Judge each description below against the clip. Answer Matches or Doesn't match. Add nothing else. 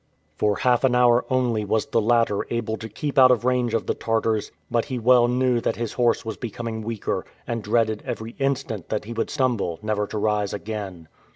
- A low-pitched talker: Matches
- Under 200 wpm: Doesn't match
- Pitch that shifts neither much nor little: Doesn't match